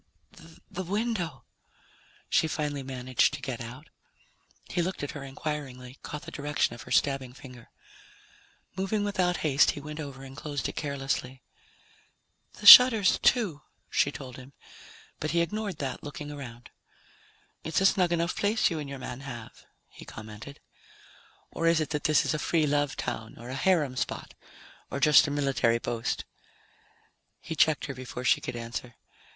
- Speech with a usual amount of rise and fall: Yes, average, 4.1 semitones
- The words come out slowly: No, average, 165 wpm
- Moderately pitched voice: Yes, medium, 145 Hz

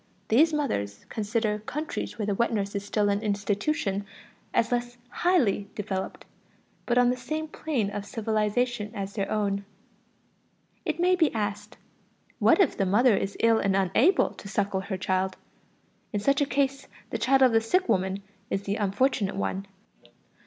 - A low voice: No, high, 210 Hz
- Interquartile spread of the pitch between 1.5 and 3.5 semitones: No, average, 4.1 semitones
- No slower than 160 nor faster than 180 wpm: Yes, average, 165 wpm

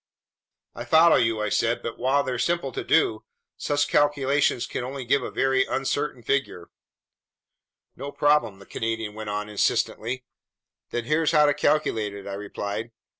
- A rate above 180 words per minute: No, average, 160 wpm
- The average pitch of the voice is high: No, low, 125 Hz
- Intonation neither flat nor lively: Yes, average, 4.8 semitones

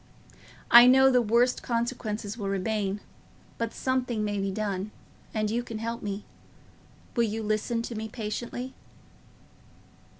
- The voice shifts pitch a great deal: No, narrow, 2.4 semitones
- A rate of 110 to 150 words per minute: Yes, slow, 135 wpm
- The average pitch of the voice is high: Yes, high, 225 Hz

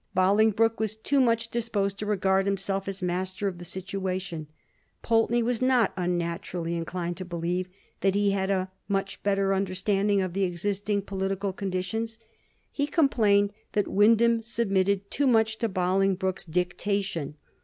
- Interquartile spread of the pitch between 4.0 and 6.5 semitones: No, average, 2.7 semitones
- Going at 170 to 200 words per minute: No, average, 145 wpm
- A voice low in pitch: No, high, 195 Hz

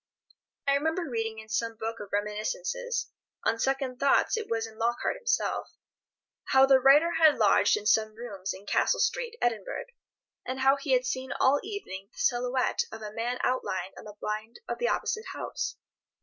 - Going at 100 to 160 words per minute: No, average, 170 wpm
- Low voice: No, very high, 250 Hz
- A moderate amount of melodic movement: Yes, average, 4.7 semitones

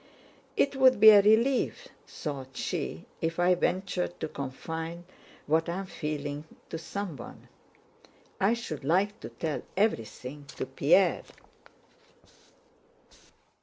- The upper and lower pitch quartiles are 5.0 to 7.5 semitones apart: Yes, average, 5.3 semitones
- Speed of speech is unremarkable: No, slow, 115 wpm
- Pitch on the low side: No, medium, 170 Hz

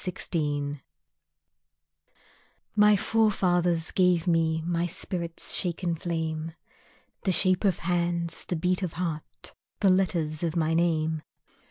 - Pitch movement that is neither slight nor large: No, narrow, 2.1 semitones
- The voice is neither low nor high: Yes, medium, 170 Hz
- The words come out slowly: Yes, slow, 115 wpm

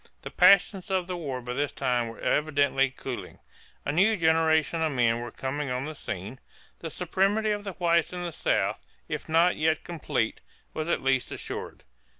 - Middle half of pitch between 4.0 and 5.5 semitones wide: Yes, average, 4.9 semitones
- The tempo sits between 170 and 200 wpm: Yes, average, 180 wpm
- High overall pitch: No, medium, 155 Hz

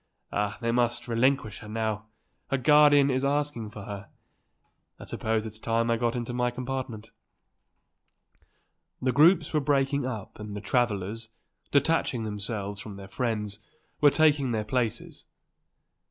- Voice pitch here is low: Yes, low, 115 Hz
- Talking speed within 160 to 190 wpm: No, average, 145 wpm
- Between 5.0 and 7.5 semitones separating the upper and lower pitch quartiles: No, average, 4.1 semitones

